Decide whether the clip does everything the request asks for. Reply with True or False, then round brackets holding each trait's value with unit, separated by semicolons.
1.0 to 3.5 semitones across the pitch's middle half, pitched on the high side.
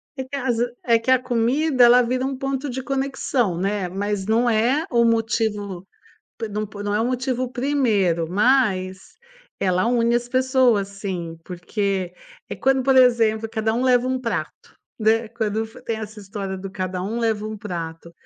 False (4.1 semitones; 225 Hz)